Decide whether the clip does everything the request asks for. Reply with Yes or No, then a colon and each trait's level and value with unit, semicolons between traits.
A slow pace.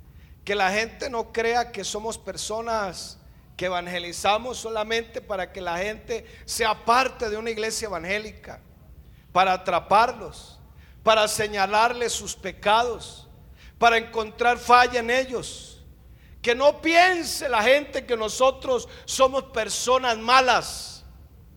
Yes: slow, 115 wpm